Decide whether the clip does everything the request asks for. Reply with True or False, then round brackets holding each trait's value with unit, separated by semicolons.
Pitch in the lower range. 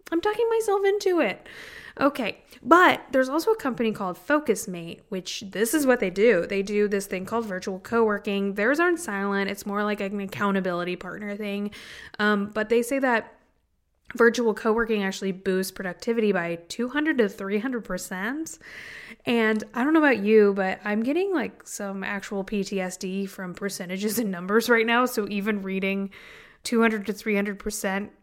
False (210 Hz)